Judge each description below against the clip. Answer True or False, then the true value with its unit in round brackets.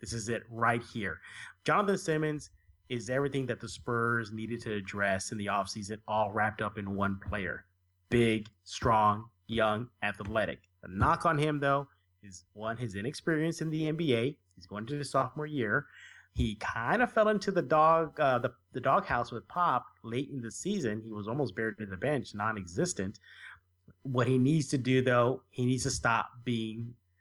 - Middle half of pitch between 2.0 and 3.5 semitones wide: False (4.7 semitones)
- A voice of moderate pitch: False (115 Hz)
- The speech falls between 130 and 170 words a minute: False (180 wpm)